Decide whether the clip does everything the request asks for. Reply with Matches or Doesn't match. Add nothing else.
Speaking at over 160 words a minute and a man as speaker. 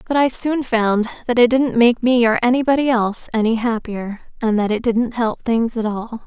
Doesn't match